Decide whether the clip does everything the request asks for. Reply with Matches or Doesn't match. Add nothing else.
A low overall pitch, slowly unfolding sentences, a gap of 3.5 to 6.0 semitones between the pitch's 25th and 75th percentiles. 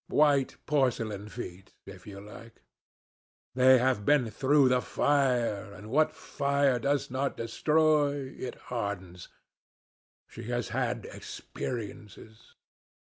Matches